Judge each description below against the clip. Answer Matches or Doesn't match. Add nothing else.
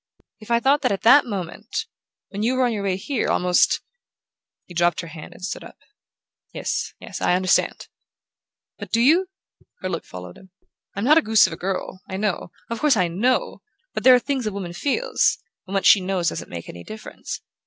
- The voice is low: Doesn't match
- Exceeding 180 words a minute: Matches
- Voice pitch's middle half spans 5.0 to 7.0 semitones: Matches